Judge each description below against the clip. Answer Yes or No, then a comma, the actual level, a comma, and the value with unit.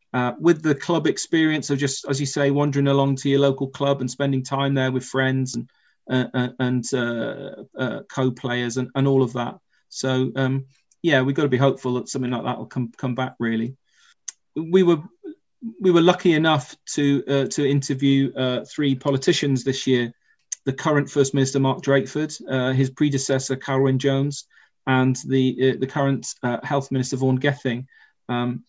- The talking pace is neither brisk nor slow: Yes, average, 180 wpm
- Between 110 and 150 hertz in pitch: Yes, low, 135 Hz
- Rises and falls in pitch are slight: Yes, narrow, 1.6 semitones